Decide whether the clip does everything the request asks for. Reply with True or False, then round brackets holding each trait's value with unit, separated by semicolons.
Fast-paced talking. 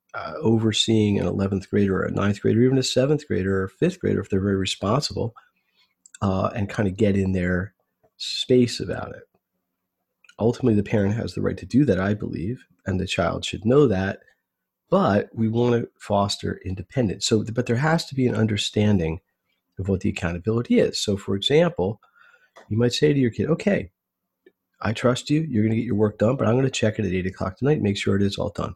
True (220 wpm)